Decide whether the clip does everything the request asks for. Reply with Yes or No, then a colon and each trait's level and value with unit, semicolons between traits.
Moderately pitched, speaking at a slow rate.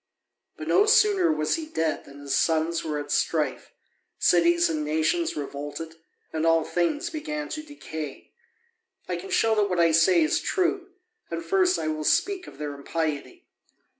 No: medium, 170 Hz; average, 165 wpm